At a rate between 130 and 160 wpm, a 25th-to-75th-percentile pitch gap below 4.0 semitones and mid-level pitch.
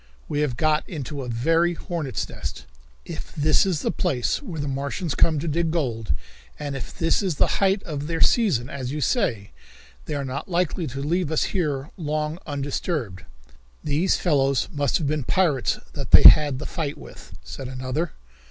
No: average, 180 wpm; average, 3.5 semitones; medium, 150 Hz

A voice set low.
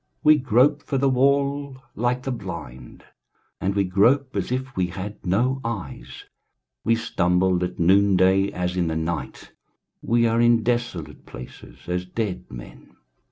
Yes: low, 100 Hz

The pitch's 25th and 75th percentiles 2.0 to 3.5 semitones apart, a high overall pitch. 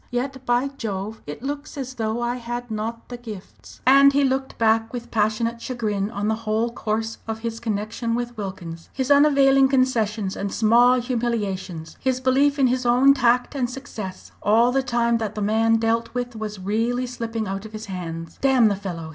Yes: average, 2.8 semitones; high, 230 Hz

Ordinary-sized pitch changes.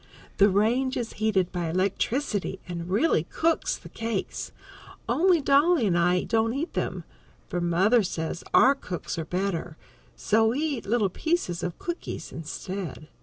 No: wide, 6.5 semitones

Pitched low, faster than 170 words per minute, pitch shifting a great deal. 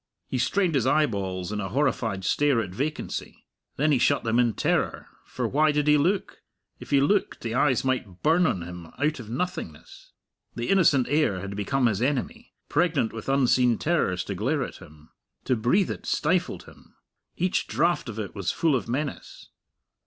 Yes: low, 130 Hz; average, 180 wpm; wide, 6.0 semitones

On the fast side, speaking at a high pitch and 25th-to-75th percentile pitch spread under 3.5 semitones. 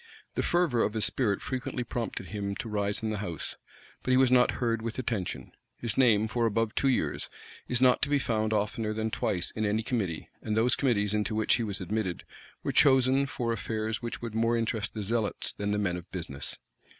No: fast, 210 wpm; low, 110 Hz; average, 2.8 semitones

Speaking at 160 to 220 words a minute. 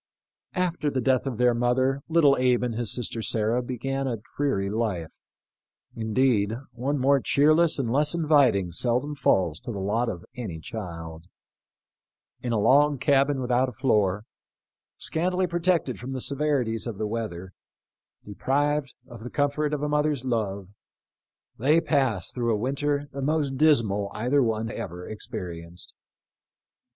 No: average, 150 wpm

